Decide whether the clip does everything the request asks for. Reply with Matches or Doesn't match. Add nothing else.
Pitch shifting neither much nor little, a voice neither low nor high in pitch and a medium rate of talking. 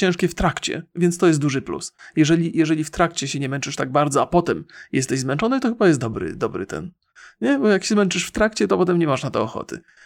Doesn't match